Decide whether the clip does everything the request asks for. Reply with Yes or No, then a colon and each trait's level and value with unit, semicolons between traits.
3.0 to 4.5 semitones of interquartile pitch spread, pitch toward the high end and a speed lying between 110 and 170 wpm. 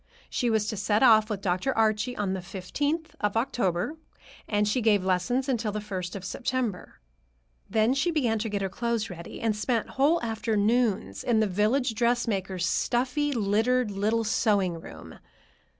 Yes: average, 3.5 semitones; high, 220 Hz; average, 165 wpm